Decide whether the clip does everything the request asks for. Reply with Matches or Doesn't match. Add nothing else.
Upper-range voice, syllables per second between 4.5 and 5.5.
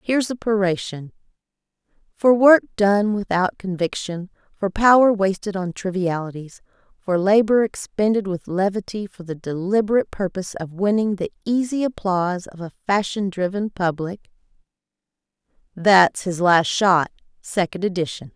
Matches